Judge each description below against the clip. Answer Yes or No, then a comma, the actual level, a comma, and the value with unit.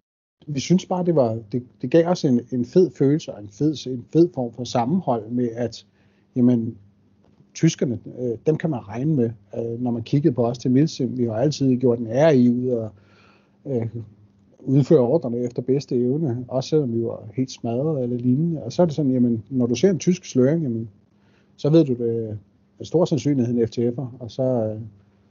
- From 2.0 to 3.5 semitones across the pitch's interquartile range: No, average, 3.9 semitones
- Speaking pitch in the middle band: No, low, 125 Hz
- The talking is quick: No, average, 205 wpm